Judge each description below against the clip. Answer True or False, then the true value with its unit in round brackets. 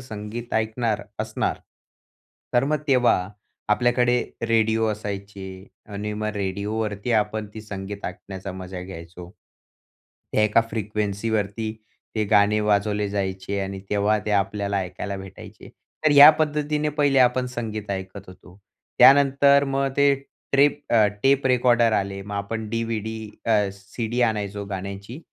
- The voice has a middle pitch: False (105 Hz)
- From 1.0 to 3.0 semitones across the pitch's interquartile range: False (3.4 semitones)